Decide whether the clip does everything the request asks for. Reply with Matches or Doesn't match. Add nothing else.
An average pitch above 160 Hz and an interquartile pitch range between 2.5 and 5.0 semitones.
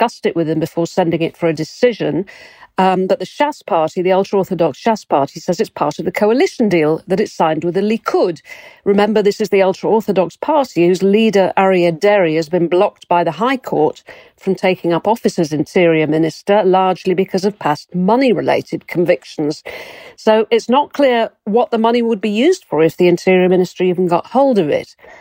Matches